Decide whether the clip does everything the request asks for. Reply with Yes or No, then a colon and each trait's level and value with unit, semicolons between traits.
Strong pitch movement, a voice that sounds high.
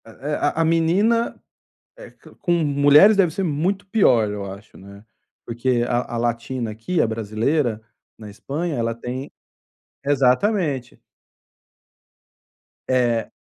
No: wide, 6.0 semitones; low, 130 Hz